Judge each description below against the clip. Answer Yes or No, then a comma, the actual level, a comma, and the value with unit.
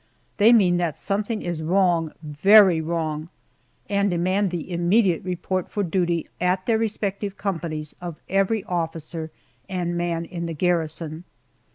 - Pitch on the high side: No, medium, 175 Hz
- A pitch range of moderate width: Yes, average, 3.0 semitones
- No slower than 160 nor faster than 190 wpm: No, average, 140 wpm